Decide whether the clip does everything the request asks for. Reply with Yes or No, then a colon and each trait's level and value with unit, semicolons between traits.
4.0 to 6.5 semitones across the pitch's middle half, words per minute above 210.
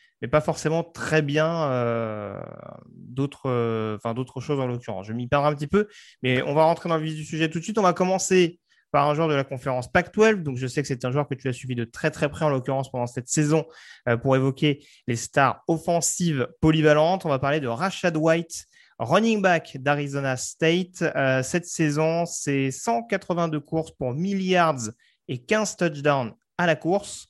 No: average, 4.4 semitones; average, 205 wpm